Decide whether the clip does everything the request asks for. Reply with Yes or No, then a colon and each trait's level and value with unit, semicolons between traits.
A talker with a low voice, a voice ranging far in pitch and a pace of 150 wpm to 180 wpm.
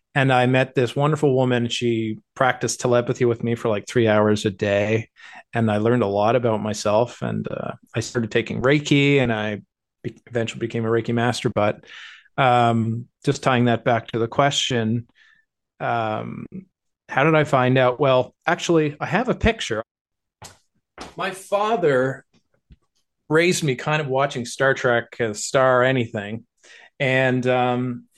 No: low, 125 Hz; average, 3.1 semitones; average, 160 wpm